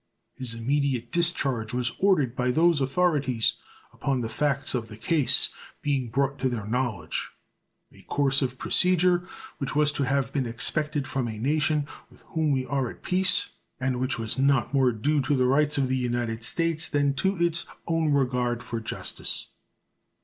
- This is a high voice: No, low, 135 Hz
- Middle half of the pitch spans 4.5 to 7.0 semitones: No, average, 3.2 semitones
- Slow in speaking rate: No, average, 170 wpm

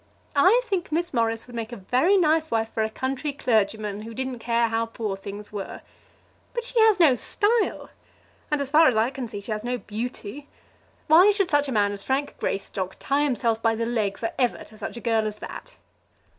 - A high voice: Yes, high, 240 Hz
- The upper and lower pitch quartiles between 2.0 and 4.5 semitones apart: No, average, 5.2 semitones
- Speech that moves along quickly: Yes, fast, 210 wpm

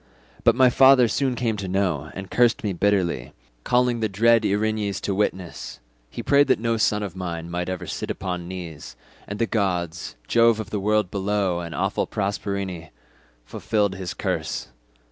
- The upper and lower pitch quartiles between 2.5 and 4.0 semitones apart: Yes, average, 3.7 semitones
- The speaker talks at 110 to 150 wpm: No, average, 165 wpm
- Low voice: Yes, low, 100 Hz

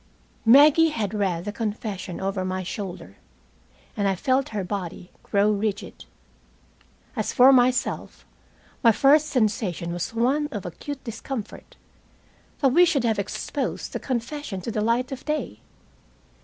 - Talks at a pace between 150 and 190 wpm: No, average, 140 wpm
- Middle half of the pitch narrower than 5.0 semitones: No, average, 5.3 semitones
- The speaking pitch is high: Yes, high, 225 Hz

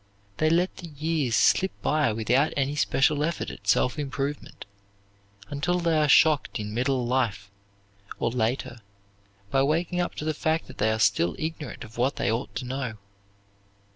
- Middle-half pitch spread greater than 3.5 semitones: Yes, average, 4.7 semitones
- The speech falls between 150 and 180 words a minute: Yes, average, 170 wpm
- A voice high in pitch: No, medium, 140 Hz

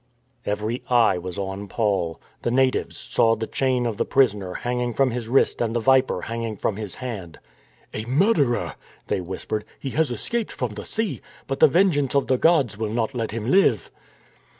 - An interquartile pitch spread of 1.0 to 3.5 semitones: No, average, 4.0 semitones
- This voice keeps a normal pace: Yes, average, 195 wpm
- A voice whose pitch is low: Yes, low, 120 Hz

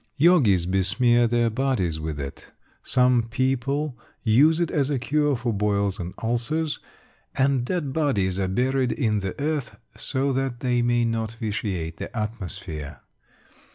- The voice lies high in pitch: No, low, 120 Hz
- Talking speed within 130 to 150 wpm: Yes, average, 145 wpm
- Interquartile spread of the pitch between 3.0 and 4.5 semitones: No, average, 5.3 semitones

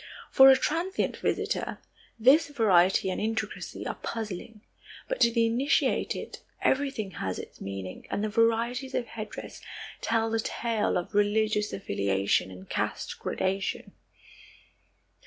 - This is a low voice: No, high, 220 Hz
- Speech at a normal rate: No, slow, 125 wpm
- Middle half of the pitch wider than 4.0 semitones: No, average, 3.6 semitones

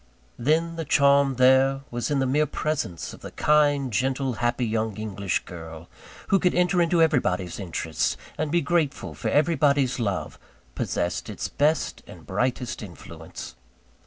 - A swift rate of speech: No, average, 150 wpm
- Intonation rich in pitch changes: Yes, wide, 5.8 semitones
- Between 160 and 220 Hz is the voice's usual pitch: No, low, 135 Hz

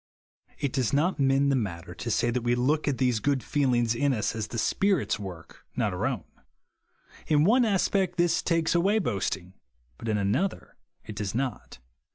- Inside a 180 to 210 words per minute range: Yes, average, 185 wpm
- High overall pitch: No, low, 130 Hz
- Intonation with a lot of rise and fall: Yes, wide, 6.5 semitones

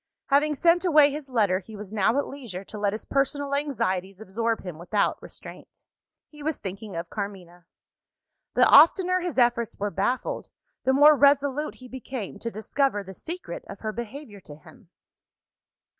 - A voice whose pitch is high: Yes, high, 235 Hz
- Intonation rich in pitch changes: Yes, wide, 6.1 semitones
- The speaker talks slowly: No, average, 165 wpm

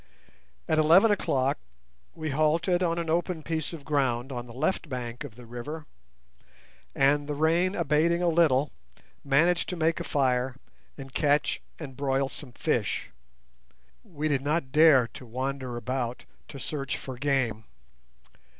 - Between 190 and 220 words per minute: No, average, 150 wpm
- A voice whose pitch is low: No, medium, 145 Hz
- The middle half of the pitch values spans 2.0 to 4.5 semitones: Yes, average, 3.7 semitones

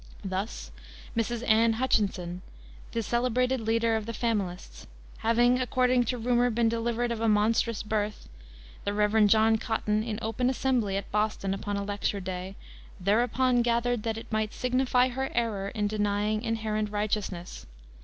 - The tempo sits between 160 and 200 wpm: No, average, 150 wpm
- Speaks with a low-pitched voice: No, high, 225 Hz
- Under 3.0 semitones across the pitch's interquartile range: Yes, narrow, 2.4 semitones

